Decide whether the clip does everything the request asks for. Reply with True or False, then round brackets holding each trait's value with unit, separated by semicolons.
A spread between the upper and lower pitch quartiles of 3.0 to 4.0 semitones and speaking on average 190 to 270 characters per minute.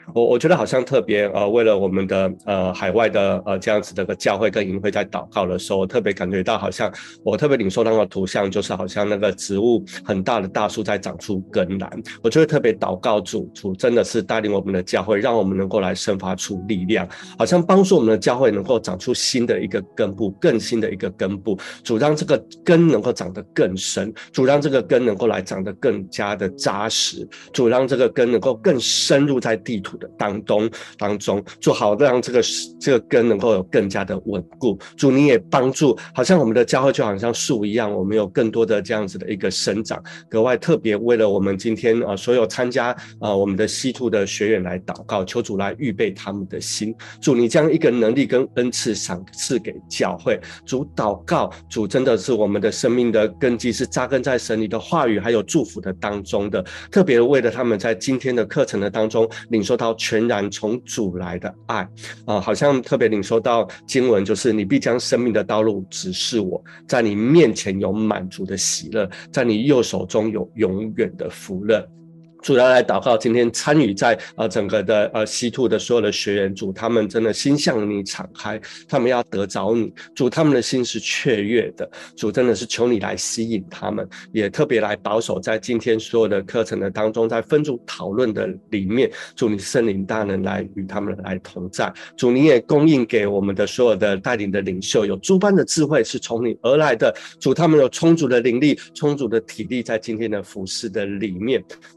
False (3.7 semitones; 305 characters per minute)